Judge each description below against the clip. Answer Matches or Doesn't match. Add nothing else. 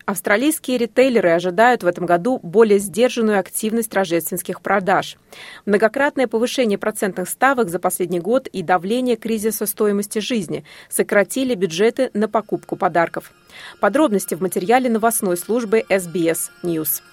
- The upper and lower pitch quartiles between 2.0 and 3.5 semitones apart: Doesn't match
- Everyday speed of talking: Matches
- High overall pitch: Matches